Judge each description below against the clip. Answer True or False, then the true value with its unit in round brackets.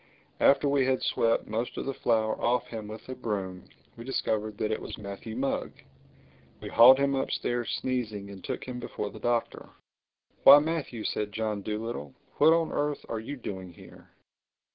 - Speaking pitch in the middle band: False (115 Hz)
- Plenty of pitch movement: False (3.7 semitones)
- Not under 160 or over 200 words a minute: True (175 wpm)